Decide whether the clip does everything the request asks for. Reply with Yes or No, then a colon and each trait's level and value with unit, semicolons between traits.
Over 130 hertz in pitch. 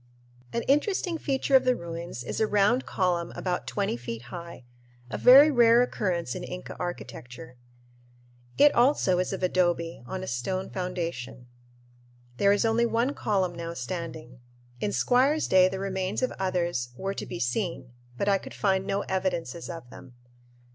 Yes: medium, 185 Hz